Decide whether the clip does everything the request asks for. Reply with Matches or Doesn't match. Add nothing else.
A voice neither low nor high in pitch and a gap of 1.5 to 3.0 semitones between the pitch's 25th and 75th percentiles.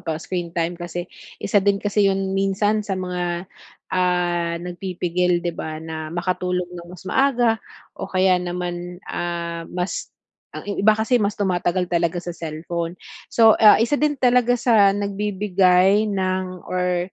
Matches